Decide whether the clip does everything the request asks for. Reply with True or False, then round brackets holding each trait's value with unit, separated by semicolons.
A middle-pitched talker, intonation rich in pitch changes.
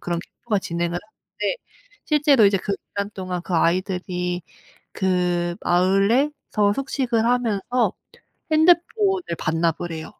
False (200 Hz; 5.8 semitones)